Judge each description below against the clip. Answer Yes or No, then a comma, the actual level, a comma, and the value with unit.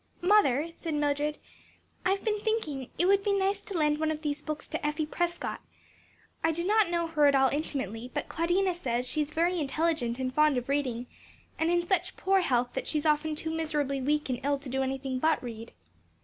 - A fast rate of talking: Yes, fast, 210 wpm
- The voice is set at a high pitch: Yes, very high, 300 Hz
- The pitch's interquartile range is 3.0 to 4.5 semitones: Yes, average, 4.1 semitones